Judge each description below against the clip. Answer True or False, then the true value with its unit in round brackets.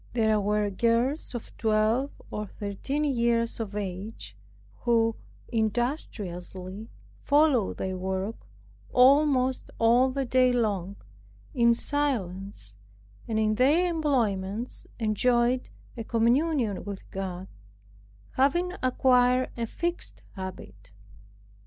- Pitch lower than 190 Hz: False (230 Hz)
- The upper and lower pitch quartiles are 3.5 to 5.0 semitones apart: True (4.2 semitones)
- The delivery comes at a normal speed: False (100 wpm)